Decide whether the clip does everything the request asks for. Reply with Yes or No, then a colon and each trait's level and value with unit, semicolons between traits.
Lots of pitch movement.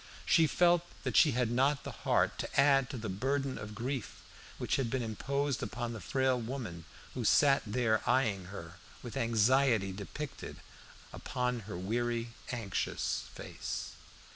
No: average, 3.8 semitones